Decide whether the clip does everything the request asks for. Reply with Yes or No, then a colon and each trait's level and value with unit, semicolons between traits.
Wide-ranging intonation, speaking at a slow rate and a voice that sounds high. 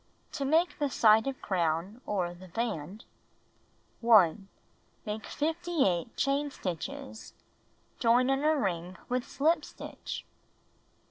Yes: wide, 7.1 semitones; slow, 115 wpm; high, 230 Hz